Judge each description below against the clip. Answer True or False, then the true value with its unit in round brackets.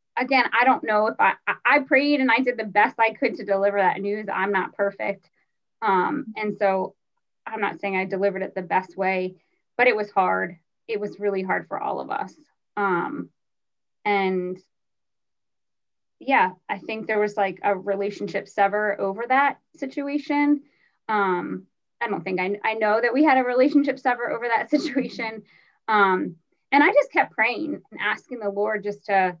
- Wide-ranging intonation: False (4.5 semitones)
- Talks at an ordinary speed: True (180 wpm)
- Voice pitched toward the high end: True (210 Hz)